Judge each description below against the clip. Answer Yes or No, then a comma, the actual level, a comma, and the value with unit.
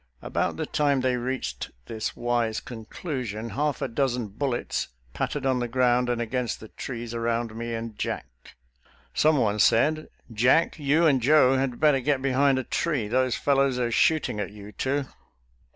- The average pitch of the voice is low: Yes, low, 125 Hz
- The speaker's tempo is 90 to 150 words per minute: No, average, 170 wpm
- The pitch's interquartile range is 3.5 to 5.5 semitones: No, average, 3.0 semitones